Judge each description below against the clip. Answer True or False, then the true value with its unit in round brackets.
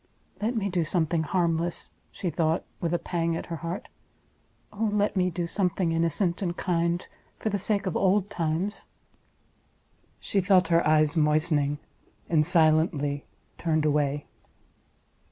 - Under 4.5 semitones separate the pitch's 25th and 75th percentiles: True (2.9 semitones)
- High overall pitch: False (170 Hz)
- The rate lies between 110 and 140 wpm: True (135 wpm)